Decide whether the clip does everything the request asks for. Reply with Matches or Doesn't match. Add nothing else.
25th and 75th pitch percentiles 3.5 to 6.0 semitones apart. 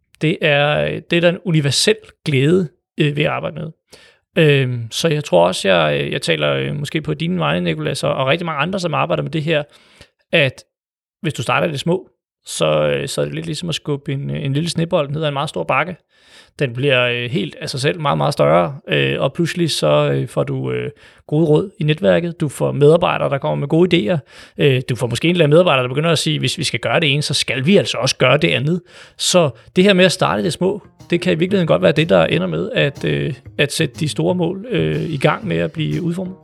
Matches